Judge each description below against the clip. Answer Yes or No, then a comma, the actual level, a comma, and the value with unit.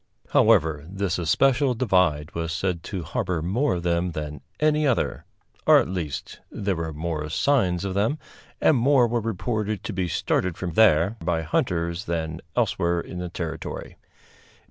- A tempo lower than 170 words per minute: Yes, average, 160 wpm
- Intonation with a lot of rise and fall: No, average, 4.8 semitones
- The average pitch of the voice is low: Yes, very low, 90 Hz